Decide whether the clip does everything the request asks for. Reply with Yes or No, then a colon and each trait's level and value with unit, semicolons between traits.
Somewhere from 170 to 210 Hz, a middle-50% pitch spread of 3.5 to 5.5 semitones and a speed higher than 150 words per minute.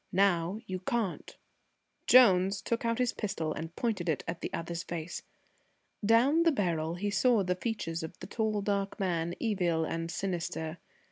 Yes: medium, 185 Hz; average, 4.6 semitones; average, 160 wpm